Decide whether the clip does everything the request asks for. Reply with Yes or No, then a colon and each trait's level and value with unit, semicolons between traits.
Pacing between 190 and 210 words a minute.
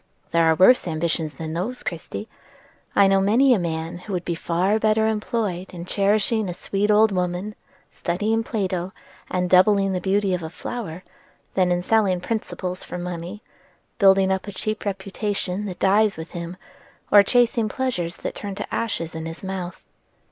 No: average, 170 wpm